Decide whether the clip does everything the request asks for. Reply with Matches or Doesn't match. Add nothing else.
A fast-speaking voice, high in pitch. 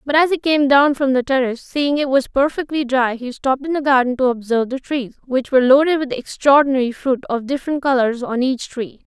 Matches